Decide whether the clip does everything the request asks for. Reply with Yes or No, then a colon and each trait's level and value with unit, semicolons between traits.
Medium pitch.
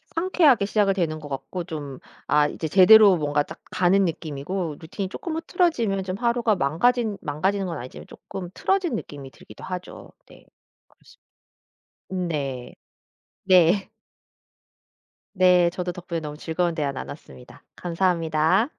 Yes: medium, 180 Hz